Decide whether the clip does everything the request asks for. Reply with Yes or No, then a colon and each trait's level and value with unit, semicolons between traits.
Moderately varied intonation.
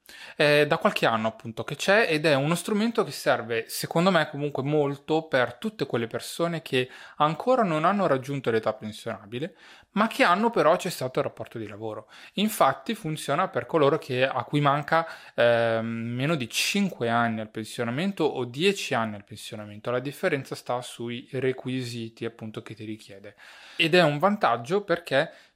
No: wide, 6.6 semitones